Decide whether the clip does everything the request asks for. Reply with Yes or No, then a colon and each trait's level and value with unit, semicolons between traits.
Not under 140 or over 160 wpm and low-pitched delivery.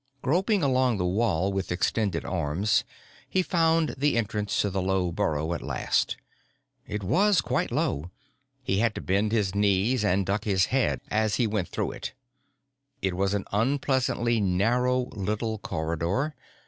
Yes: average, 155 wpm; low, 105 Hz